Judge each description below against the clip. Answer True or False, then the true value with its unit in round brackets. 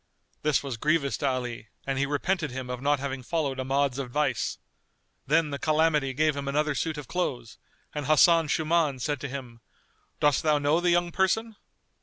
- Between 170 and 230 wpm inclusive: True (180 wpm)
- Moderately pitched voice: True (145 Hz)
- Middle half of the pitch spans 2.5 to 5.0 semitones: True (2.8 semitones)